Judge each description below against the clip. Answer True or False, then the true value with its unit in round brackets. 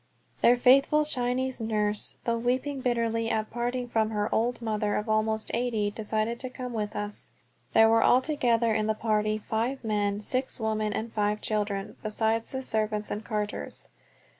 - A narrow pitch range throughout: True (2.3 semitones)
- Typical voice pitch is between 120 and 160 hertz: False (225 Hz)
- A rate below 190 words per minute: True (165 wpm)